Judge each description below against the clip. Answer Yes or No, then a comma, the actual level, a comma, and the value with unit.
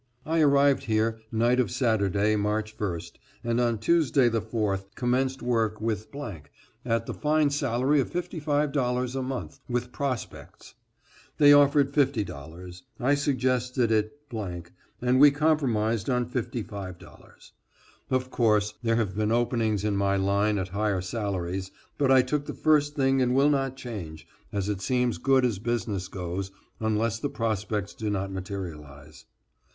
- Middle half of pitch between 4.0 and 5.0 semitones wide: Yes, average, 4.6 semitones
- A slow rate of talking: No, average, 145 wpm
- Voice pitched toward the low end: Yes, low, 115 Hz